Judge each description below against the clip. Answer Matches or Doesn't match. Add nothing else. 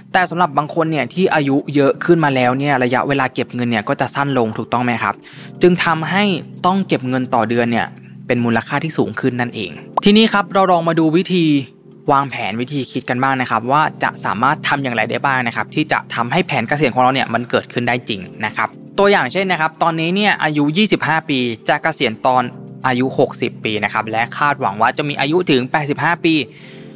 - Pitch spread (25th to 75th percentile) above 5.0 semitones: Matches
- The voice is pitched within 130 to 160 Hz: Matches